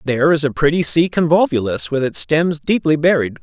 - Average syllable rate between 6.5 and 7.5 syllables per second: No, 5.5 syllables/s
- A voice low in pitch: No, medium, 150 Hz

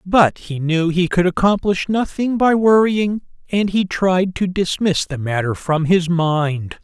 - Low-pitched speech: No, medium, 180 Hz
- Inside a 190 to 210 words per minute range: No, average, 165 wpm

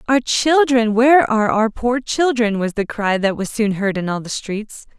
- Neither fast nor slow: No, fast, 215 wpm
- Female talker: Yes, female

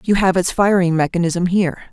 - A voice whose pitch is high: No, medium, 180 Hz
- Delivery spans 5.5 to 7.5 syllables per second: Yes, 5.7 syllables/s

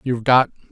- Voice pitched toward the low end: Yes, low, 120 Hz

